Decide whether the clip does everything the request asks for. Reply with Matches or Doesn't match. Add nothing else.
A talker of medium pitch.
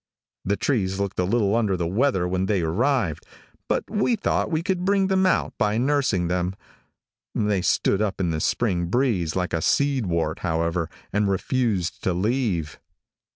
Doesn't match